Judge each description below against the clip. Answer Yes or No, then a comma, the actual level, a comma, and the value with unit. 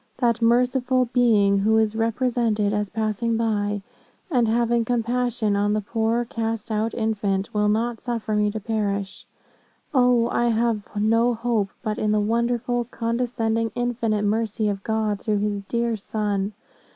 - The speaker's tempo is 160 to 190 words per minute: No, average, 150 wpm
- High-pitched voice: Yes, high, 225 Hz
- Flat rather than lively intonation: Yes, narrow, 2.2 semitones